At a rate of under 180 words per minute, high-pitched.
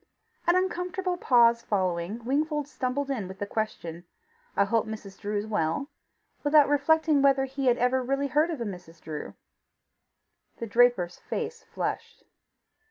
Yes: average, 150 wpm; high, 245 Hz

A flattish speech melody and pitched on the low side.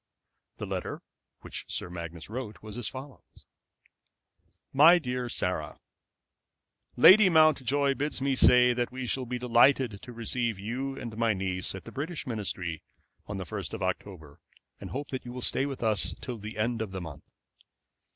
No: average, 4.6 semitones; low, 120 Hz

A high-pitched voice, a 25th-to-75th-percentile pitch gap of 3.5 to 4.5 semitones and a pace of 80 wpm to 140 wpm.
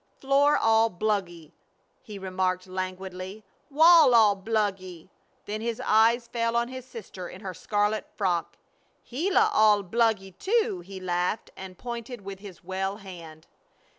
Yes: high, 205 Hz; average, 3.9 semitones; slow, 135 wpm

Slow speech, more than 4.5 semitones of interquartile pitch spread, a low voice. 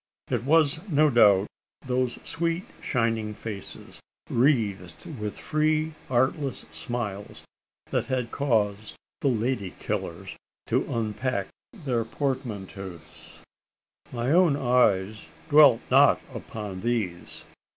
Yes: slow, 100 wpm; average, 5.1 semitones; low, 120 Hz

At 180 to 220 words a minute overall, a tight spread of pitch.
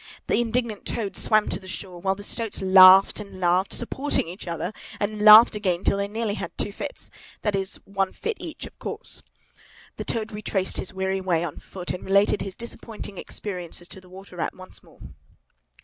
Yes: average, 185 wpm; narrow, 2.3 semitones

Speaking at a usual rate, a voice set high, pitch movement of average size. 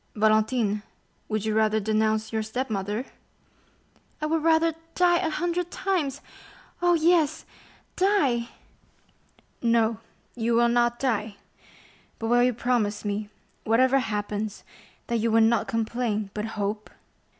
No: slow, 120 wpm; high, 230 Hz; average, 3.9 semitones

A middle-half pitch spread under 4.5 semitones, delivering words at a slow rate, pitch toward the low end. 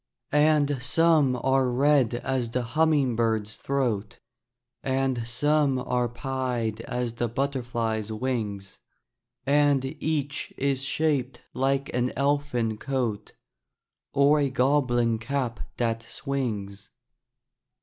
Yes: average, 3.1 semitones; slow, 105 wpm; low, 130 Hz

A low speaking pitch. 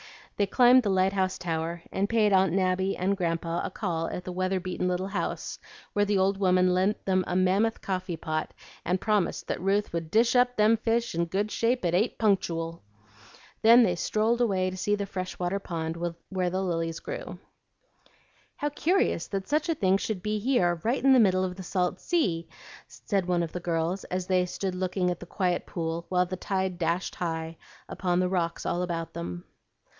No: medium, 185 Hz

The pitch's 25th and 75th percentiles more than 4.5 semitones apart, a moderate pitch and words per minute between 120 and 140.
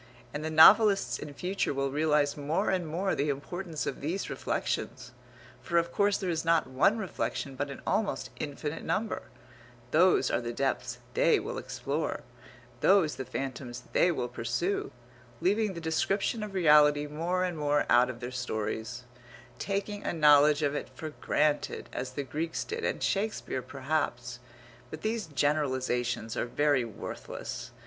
No: average, 5.3 semitones; medium, 150 Hz; average, 155 wpm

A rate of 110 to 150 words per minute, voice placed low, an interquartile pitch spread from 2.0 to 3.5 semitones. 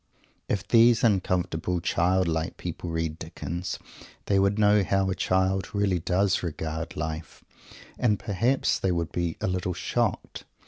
Yes: average, 140 wpm; very low, 90 Hz; average, 2.8 semitones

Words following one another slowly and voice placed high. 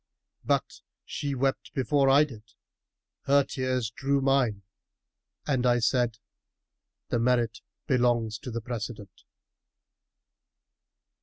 No: slow, 105 wpm; low, 125 Hz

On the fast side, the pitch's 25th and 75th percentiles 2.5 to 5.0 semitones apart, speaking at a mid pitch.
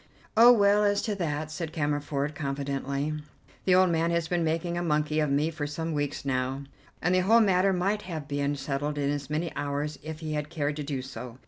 Yes: fast, 215 wpm; average, 3.2 semitones; medium, 150 Hz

